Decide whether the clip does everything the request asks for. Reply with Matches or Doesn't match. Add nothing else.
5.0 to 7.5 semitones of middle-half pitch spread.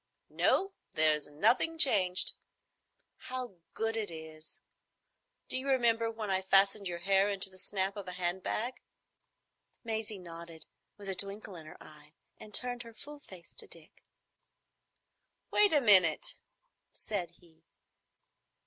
Doesn't match